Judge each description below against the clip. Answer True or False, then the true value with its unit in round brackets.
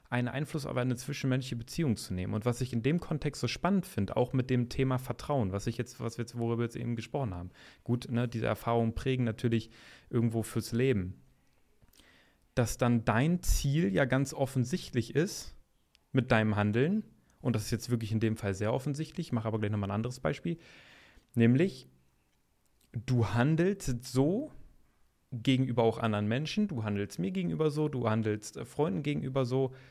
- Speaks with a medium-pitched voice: False (120 Hz)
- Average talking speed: True (180 wpm)